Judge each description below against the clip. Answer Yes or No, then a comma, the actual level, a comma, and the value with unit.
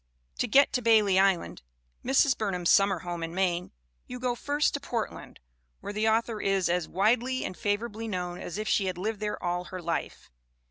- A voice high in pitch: Yes, high, 205 Hz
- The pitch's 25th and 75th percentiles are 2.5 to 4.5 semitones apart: Yes, average, 4.2 semitones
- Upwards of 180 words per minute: Yes, average, 190 wpm